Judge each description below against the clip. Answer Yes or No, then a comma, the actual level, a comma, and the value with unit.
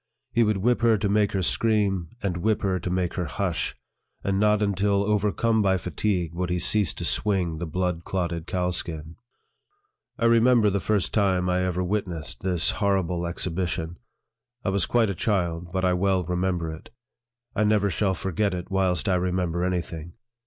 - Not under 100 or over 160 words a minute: No, average, 180 wpm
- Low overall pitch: Yes, very low, 95 Hz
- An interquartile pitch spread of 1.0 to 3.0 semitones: Yes, average, 2.7 semitones